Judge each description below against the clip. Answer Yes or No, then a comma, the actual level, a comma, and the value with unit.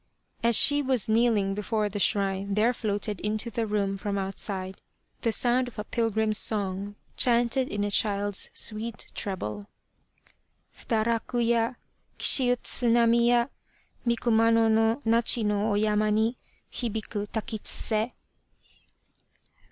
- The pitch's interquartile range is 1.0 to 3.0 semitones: Yes, narrow, 2.4 semitones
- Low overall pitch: No, high, 220 Hz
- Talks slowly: Yes, slow, 125 wpm